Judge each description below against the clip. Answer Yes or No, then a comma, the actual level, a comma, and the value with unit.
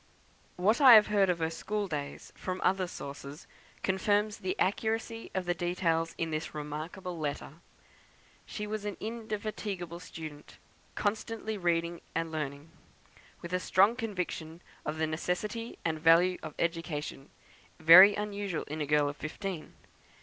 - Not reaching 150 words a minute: Yes, average, 140 wpm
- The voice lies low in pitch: No, medium, 175 Hz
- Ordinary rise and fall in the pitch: Yes, average, 4.5 semitones